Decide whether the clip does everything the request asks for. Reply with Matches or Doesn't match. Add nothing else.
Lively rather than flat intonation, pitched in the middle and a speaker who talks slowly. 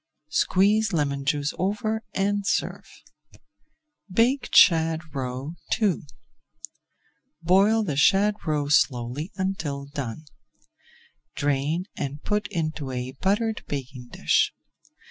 Matches